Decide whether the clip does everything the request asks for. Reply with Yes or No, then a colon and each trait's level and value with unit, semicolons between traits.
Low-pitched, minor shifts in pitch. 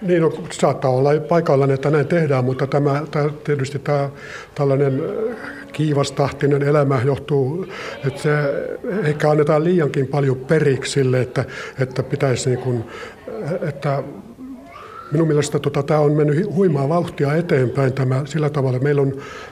No: medium, 145 Hz; narrow, 2.1 semitones